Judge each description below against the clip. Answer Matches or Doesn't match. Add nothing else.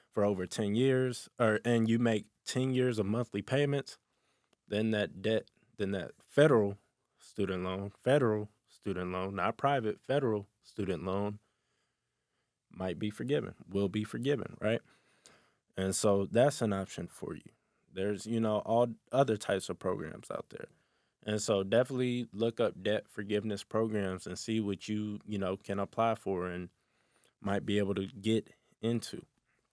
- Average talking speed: Matches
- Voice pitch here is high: Doesn't match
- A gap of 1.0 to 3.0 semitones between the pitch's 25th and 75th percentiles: Matches